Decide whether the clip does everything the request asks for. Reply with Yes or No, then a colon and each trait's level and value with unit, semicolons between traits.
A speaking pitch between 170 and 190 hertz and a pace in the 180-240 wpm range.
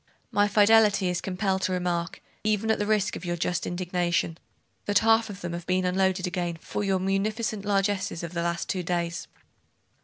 Yes: medium, 185 Hz; average, 185 wpm